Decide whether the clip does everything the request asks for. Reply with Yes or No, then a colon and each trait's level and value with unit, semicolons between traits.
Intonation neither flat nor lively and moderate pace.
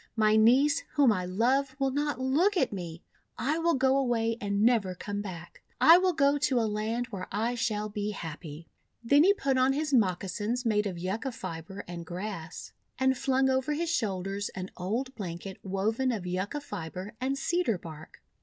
No: wide, 5.8 semitones; average, 180 wpm